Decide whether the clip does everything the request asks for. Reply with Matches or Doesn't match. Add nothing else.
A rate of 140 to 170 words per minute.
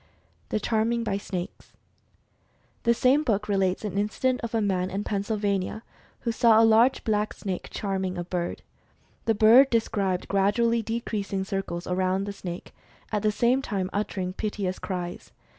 Matches